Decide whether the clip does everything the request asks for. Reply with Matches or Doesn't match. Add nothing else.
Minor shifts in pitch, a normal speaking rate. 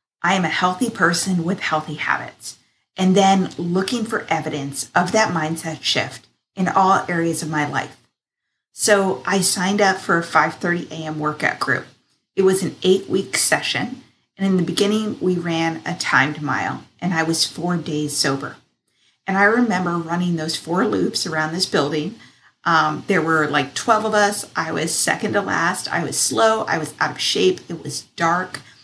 Doesn't match